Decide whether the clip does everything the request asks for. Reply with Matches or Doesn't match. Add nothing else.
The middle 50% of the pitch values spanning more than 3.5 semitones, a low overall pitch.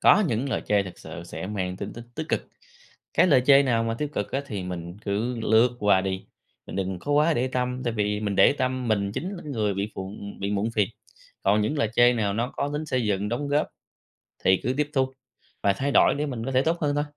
Matches